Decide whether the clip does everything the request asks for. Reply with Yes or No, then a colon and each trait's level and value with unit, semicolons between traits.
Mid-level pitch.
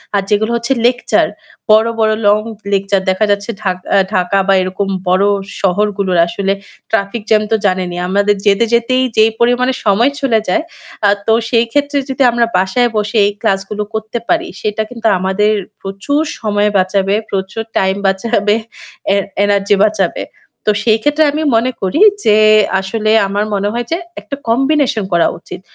No: high, 210 Hz